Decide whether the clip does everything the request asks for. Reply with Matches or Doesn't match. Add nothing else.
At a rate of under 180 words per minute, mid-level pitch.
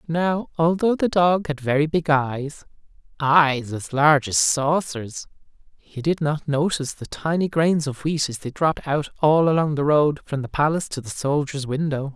Doesn't match